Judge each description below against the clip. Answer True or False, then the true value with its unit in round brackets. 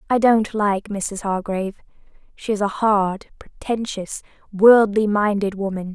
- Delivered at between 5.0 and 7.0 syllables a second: False (4.2 syllables/s)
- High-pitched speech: True (205 Hz)